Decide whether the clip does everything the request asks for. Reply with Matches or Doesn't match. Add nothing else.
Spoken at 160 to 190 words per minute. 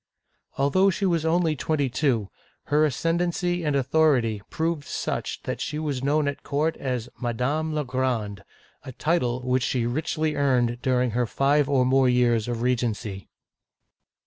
Matches